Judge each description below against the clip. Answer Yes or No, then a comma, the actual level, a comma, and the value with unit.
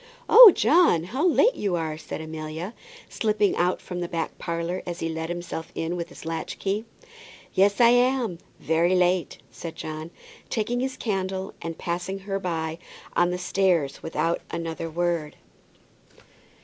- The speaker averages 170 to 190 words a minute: No, average, 155 wpm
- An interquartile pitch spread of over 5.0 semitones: No, average, 3.3 semitones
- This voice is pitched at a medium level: Yes, medium, 175 Hz